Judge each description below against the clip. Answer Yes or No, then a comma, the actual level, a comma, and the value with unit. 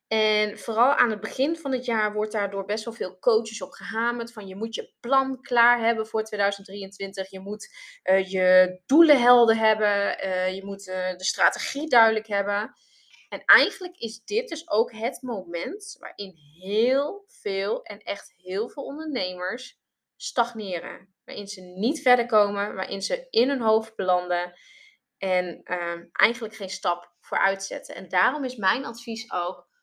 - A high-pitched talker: Yes, high, 215 Hz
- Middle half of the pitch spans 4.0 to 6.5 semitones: Yes, average, 4.3 semitones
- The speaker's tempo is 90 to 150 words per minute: No, average, 165 wpm